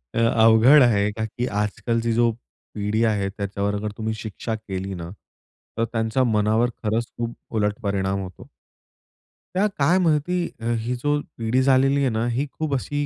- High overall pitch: No, low, 115 Hz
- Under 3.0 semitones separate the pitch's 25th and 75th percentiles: No, average, 3.7 semitones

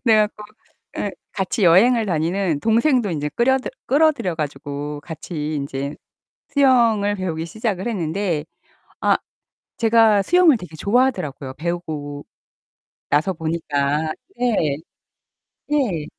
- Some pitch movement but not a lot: No, wide, 7.0 semitones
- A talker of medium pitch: Yes, medium, 180 Hz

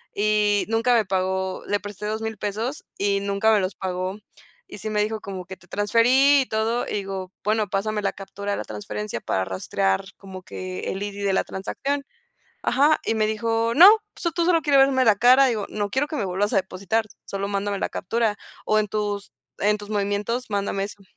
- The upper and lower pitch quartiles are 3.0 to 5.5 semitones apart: No, narrow, 2.6 semitones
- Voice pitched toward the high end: Yes, high, 205 Hz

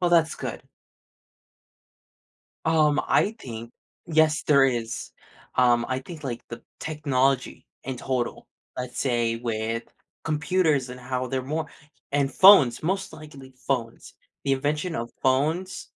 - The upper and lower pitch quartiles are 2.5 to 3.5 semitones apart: No, average, 3.9 semitones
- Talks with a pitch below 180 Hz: Yes, low, 135 Hz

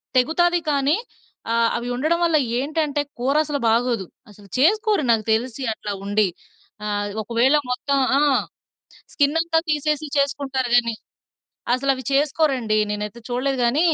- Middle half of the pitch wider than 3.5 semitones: Yes, average, 4.5 semitones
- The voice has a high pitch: Yes, very high, 270 Hz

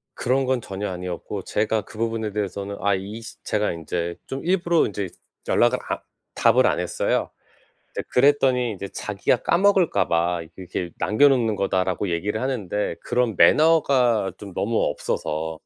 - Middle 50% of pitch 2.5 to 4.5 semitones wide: No, average, 5.1 semitones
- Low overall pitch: Yes, low, 105 Hz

